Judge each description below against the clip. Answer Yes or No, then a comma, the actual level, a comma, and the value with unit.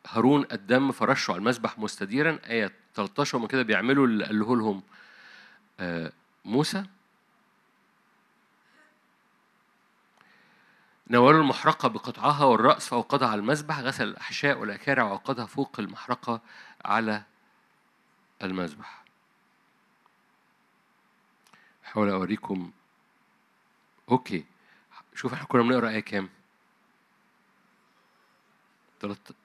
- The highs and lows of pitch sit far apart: No, average, 4.9 semitones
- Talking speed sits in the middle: Yes, average, 75 wpm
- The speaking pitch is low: Yes, low, 115 Hz